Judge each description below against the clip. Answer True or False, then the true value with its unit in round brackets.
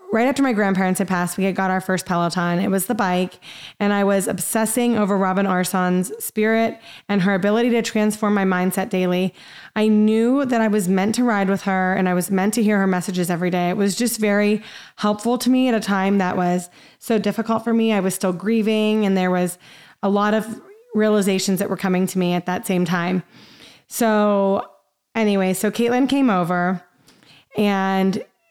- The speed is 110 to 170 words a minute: False (200 wpm)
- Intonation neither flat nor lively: True (3.0 semitones)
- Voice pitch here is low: False (200 Hz)